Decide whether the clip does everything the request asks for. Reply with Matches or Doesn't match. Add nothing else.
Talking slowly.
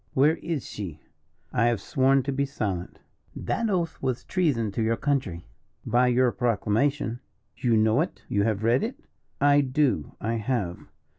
Doesn't match